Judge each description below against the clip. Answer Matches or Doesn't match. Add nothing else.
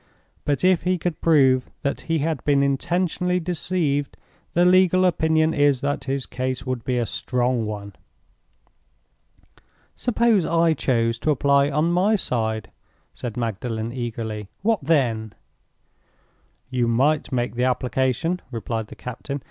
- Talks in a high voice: Doesn't match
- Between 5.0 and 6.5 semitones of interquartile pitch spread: Matches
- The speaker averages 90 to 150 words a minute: Matches